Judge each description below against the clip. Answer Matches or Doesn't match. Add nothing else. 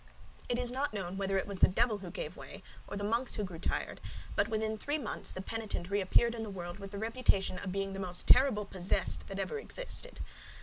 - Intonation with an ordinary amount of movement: Matches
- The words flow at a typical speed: Doesn't match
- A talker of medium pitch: Doesn't match